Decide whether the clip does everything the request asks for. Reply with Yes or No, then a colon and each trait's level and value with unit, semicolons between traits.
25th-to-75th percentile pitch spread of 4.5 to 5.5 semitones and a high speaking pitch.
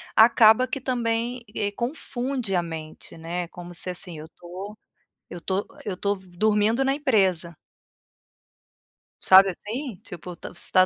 Yes: average, 5.0 semitones; high, 200 Hz